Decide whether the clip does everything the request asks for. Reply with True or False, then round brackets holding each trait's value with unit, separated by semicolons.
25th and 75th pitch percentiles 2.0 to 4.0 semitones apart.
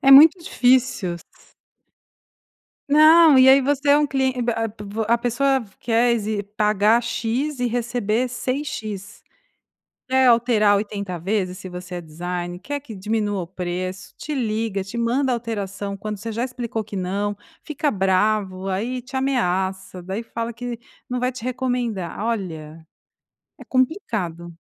False (4.8 semitones)